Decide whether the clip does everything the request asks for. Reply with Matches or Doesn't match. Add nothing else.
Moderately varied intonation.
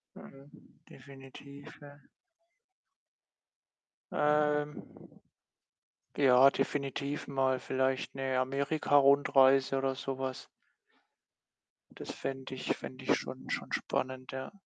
Doesn't match